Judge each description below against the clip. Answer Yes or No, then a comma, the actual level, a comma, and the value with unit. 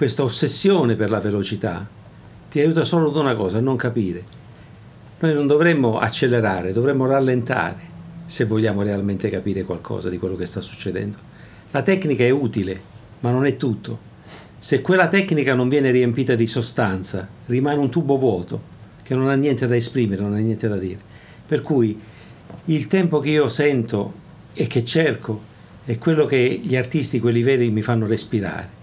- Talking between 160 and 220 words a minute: Yes, fast, 170 wpm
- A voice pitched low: Yes, low, 120 Hz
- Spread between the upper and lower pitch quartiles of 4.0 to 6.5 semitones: Yes, average, 5.1 semitones